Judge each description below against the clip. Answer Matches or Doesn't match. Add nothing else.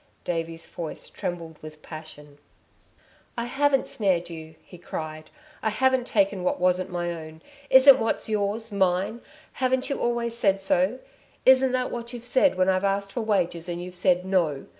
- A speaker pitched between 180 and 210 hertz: Matches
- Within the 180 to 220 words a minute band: Doesn't match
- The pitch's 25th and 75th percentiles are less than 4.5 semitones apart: Doesn't match